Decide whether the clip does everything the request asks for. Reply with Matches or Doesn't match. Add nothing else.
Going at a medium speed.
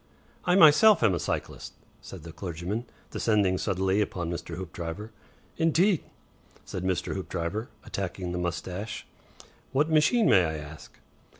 Doesn't match